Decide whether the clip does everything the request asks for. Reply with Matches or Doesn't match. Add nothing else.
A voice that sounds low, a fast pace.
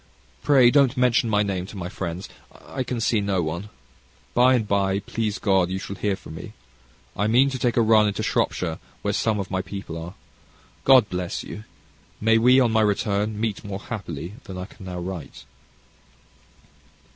Doesn't match